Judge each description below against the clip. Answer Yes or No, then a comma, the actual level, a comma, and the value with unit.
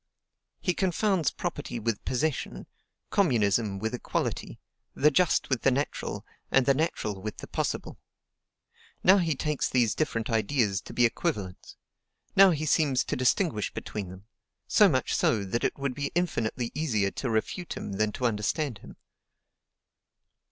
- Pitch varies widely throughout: Yes, wide, 6.3 semitones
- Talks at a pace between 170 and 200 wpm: No, average, 150 wpm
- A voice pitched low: Yes, low, 125 Hz